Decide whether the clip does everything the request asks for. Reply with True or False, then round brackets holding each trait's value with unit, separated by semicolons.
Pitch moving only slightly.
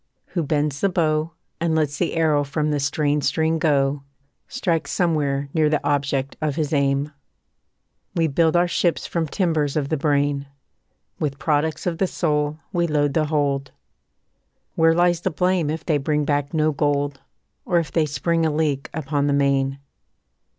True (2.3 semitones)